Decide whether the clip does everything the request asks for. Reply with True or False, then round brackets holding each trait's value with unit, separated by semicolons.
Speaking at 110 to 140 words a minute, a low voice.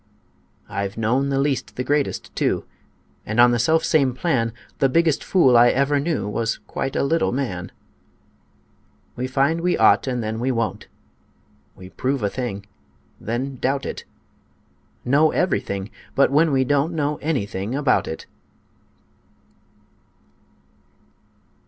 True (135 wpm; 130 Hz)